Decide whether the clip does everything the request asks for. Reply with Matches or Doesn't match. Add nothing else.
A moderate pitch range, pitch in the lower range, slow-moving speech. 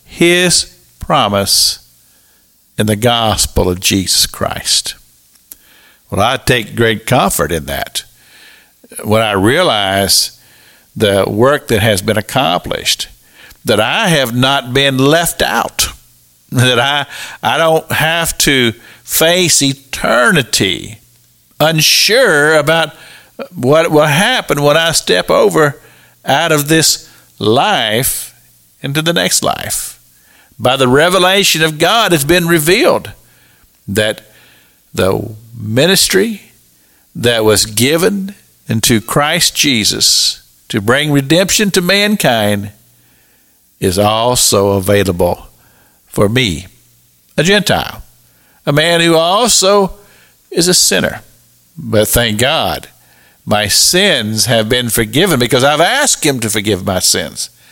Doesn't match